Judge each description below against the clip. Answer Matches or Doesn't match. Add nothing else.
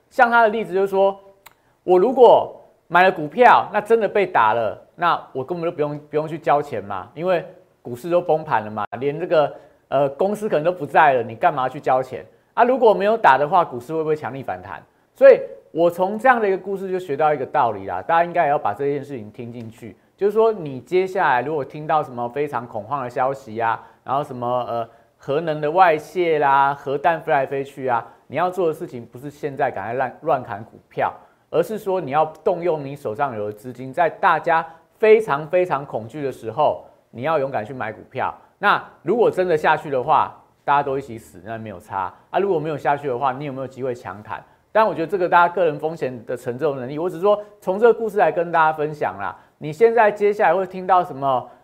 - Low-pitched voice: Doesn't match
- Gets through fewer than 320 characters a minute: Doesn't match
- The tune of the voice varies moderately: Doesn't match